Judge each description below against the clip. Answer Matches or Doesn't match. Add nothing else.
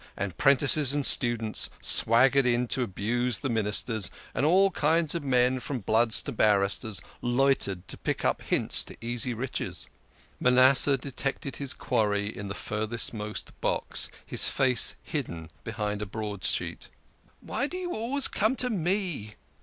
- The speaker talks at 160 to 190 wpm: Doesn't match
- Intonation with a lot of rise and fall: Doesn't match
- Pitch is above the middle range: Doesn't match